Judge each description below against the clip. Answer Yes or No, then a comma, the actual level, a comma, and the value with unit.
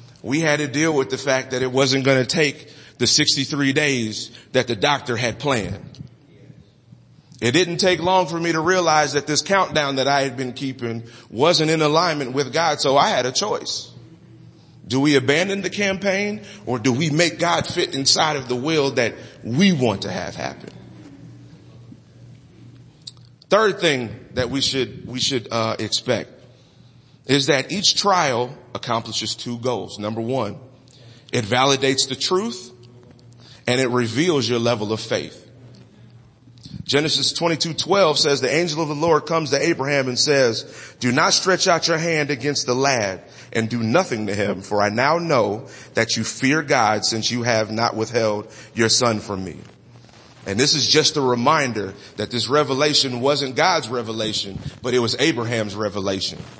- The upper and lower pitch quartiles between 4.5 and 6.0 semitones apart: No, average, 4.1 semitones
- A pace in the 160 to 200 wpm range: Yes, average, 170 wpm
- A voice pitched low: Yes, low, 130 Hz